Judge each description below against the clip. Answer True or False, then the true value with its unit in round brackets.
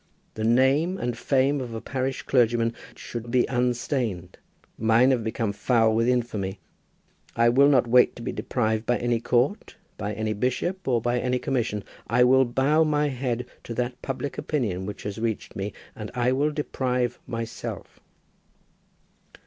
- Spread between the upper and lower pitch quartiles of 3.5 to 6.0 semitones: False (2.6 semitones)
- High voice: False (120 Hz)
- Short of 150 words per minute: False (160 wpm)